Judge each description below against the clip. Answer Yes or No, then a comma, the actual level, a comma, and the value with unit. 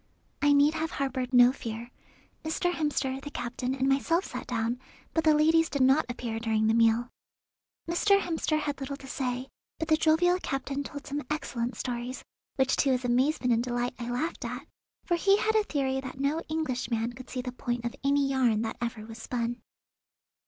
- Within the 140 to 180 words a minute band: No, average, 190 wpm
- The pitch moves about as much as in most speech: Yes, average, 3.8 semitones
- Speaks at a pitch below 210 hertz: No, very high, 265 Hz